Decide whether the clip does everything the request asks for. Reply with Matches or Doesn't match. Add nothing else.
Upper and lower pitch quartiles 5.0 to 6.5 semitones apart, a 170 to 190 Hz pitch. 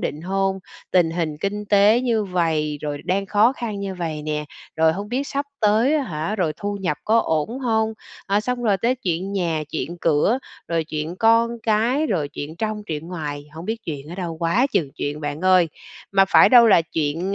Matches